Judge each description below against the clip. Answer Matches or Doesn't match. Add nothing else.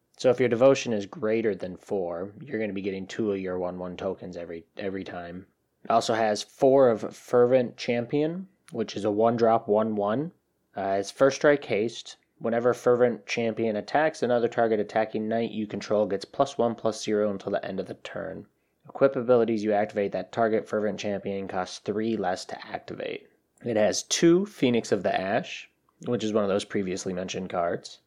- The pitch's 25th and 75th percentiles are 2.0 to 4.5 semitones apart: Matches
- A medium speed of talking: Matches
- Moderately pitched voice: Doesn't match